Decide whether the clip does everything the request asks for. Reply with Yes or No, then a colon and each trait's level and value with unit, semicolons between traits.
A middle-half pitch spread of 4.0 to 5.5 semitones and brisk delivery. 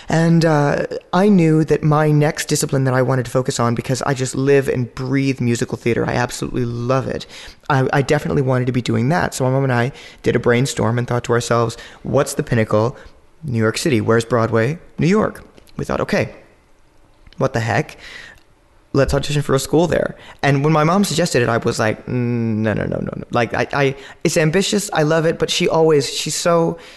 Yes: average, 4.4 semitones; fast, 215 wpm